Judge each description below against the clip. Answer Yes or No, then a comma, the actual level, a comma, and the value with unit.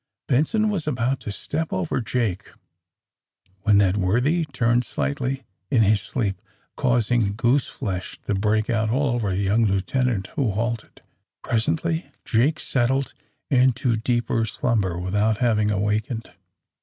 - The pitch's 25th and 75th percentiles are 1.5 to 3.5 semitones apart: No, average, 3.9 semitones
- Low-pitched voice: Yes, low, 115 Hz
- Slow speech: Yes, slow, 130 wpm